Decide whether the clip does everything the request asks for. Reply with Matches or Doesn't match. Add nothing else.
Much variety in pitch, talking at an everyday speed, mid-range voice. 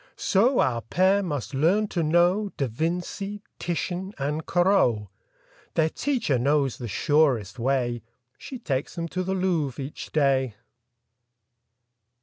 Doesn't match